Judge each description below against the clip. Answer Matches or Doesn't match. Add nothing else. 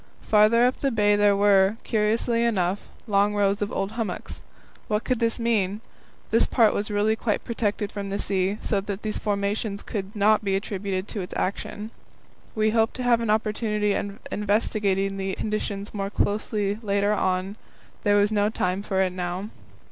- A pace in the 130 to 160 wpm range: Doesn't match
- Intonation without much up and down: Matches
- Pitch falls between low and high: Doesn't match